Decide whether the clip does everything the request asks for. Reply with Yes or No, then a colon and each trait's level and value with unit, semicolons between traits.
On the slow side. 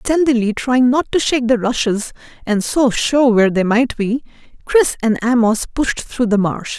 No: average, 185 wpm